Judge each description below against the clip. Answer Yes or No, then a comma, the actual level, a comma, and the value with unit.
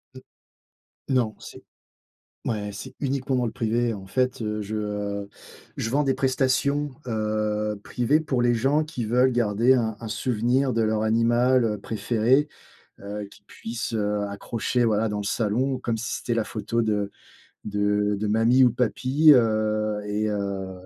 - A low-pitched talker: Yes, low, 115 Hz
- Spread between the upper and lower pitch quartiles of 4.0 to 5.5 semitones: No, average, 3.2 semitones